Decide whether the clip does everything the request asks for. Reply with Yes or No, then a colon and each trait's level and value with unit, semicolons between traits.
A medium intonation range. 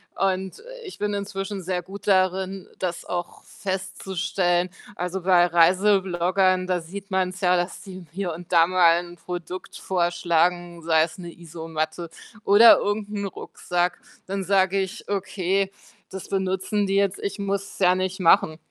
No: narrow, 1.9 semitones